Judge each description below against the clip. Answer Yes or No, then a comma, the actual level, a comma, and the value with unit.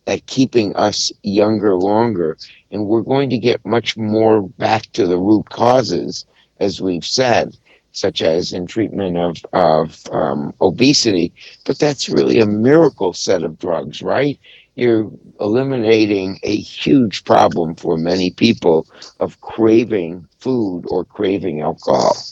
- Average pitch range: Yes, average, 3.7 semitones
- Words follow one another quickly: No, slow, 135 wpm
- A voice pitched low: Yes, low, 110 Hz